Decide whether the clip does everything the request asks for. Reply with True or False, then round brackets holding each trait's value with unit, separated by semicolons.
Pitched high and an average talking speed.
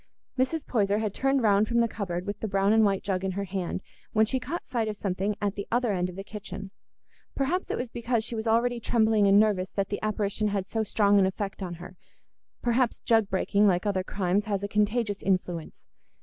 False (205 Hz; 220 wpm)